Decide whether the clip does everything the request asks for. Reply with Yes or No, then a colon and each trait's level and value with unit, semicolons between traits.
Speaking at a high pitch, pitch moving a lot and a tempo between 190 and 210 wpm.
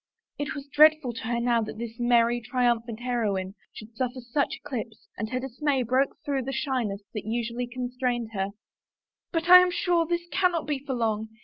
No: high, 245 Hz; average, 3.4 semitones; average, 195 wpm